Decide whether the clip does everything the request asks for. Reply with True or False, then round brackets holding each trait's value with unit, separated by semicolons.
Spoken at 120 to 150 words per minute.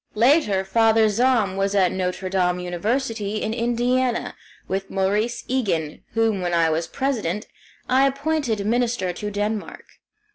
True (135 wpm)